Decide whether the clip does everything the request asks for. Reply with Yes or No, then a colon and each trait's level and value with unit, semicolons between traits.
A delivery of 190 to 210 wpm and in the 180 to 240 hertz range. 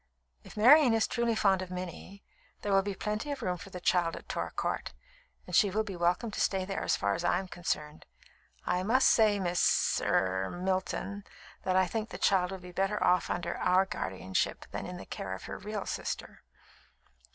Yes: fast, 205 wpm; high, 190 Hz